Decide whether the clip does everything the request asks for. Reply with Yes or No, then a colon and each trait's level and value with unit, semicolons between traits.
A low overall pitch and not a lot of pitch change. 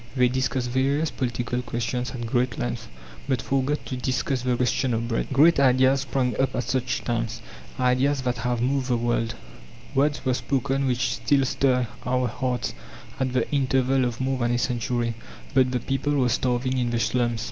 Yes: low, 125 Hz; narrow, 1.6 semitones